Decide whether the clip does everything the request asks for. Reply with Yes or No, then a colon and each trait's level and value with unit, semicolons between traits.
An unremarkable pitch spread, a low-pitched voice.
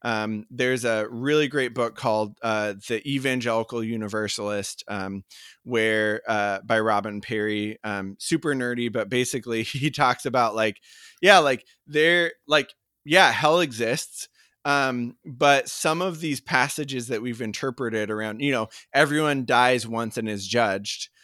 Yes: average, 4.4 semitones; low, 120 Hz